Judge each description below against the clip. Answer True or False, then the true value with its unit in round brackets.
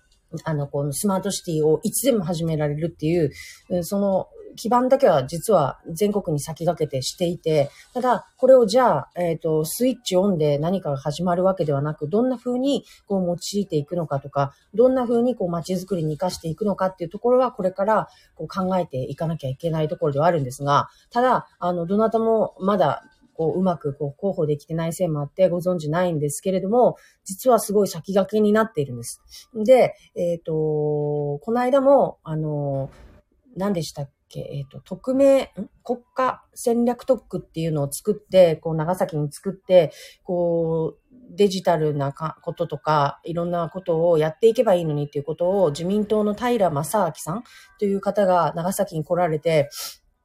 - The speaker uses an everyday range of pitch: True (5.0 semitones)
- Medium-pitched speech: True (175 Hz)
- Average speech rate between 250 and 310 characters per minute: False (365 characters per minute)